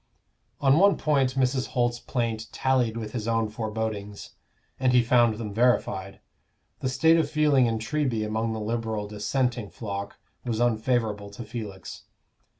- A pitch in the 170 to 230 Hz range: No, low, 115 Hz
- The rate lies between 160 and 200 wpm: No, average, 150 wpm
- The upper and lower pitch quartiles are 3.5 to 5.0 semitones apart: No, average, 2.9 semitones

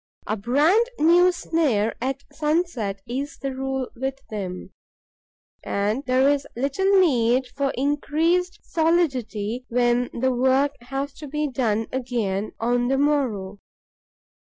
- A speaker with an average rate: No, slow, 125 wpm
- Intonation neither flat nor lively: Yes, average, 3.9 semitones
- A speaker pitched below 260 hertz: No, very high, 265 Hz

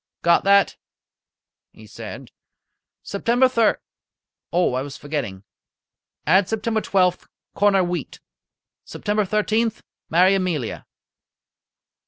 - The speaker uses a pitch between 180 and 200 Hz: Yes, high, 190 Hz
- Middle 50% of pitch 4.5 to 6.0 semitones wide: No, average, 4.1 semitones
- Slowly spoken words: Yes, slow, 95 wpm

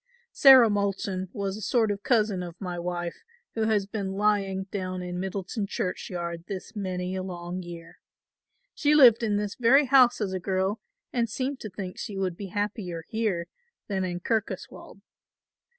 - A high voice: Yes, high, 195 Hz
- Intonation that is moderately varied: Yes, average, 3.1 semitones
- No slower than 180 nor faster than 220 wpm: No, average, 165 wpm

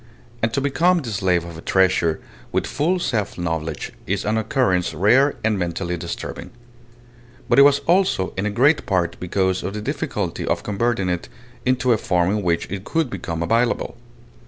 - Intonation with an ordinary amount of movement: No, wide, 6.1 semitones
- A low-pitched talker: Yes, low, 100 Hz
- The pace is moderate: Yes, average, 180 wpm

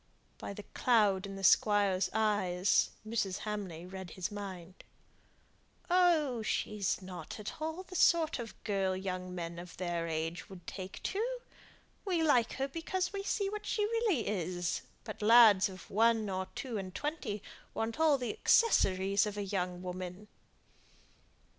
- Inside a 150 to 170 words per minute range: Yes, average, 155 wpm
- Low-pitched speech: No, high, 205 Hz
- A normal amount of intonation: No, wide, 6.6 semitones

